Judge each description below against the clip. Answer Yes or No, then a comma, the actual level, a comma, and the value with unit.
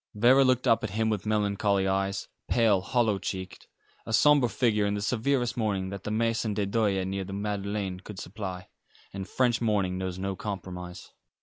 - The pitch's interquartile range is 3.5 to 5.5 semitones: No, average, 2.8 semitones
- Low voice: Yes, low, 105 Hz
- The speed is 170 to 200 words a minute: Yes, average, 180 wpm